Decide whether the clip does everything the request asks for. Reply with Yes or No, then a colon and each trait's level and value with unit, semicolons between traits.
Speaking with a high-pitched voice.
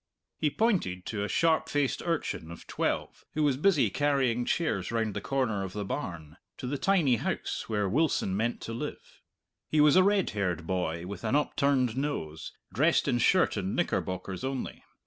No: low, 120 Hz